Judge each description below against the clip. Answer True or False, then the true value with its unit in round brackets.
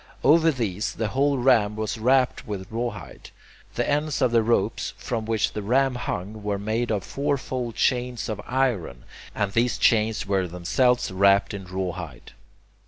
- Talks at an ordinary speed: True (160 wpm)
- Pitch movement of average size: True (4.0 semitones)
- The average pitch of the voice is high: False (110 Hz)